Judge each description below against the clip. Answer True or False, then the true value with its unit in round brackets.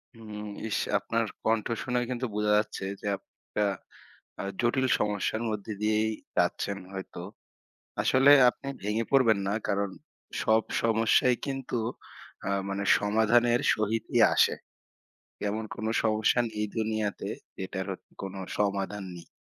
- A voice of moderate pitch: False (110 Hz)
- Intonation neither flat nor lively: False (2.2 semitones)